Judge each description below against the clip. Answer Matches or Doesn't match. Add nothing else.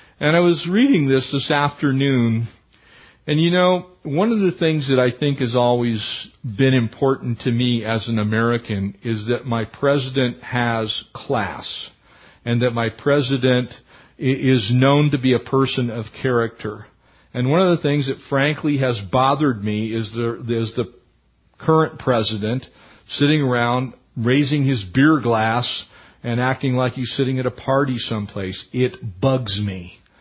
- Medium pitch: Doesn't match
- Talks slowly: Doesn't match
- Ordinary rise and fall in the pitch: Matches